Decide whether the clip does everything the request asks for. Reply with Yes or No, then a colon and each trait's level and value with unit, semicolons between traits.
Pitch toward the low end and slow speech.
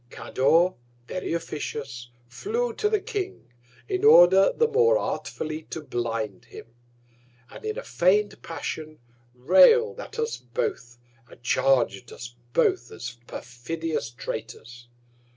No: medium, 160 Hz; slow, 120 wpm